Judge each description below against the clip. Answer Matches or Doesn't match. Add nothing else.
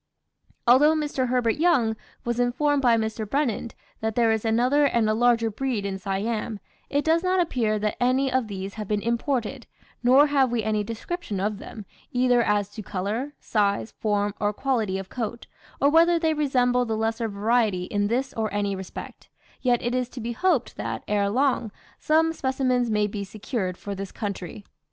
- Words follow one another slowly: Doesn't match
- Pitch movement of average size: Matches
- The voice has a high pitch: Matches